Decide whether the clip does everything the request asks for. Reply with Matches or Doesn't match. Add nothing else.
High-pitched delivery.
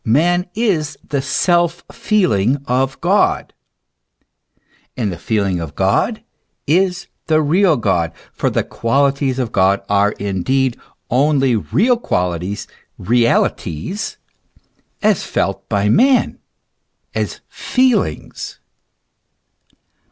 Doesn't match